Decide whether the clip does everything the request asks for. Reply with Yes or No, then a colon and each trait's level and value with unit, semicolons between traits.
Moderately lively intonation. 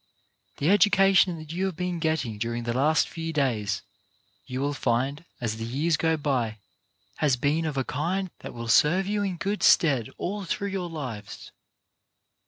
No: wide, 6.2 semitones